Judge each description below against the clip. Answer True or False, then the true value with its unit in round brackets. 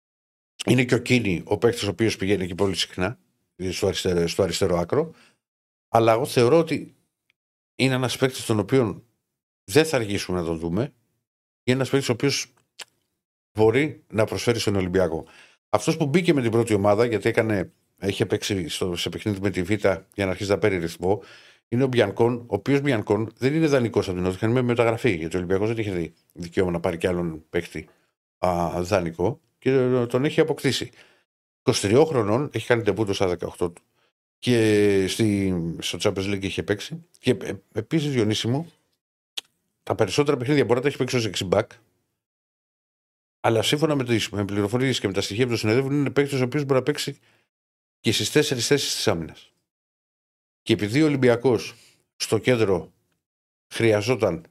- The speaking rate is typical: False (175 wpm)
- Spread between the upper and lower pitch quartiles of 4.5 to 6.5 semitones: True (5.2 semitones)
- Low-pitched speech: True (115 Hz)